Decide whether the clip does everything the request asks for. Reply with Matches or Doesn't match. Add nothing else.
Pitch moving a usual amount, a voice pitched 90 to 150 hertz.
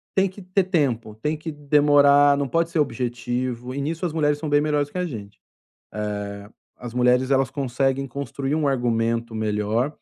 Matches